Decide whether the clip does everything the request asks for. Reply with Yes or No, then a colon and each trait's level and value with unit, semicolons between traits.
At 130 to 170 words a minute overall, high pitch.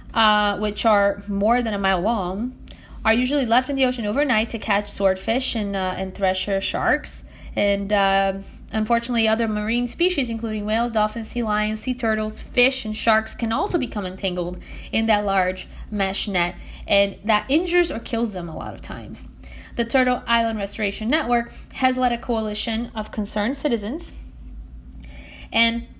Yes: average, 165 wpm; high, 215 Hz